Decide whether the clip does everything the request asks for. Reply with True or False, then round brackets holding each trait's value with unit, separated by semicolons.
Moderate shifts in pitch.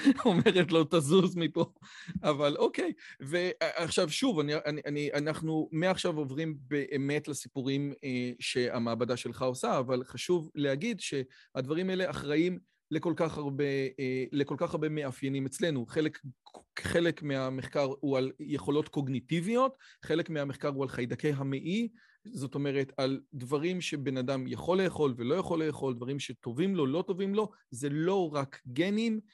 True (3.9 semitones)